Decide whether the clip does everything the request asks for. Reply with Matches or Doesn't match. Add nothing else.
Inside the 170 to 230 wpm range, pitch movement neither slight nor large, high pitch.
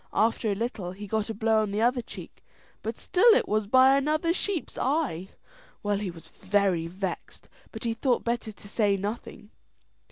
Matches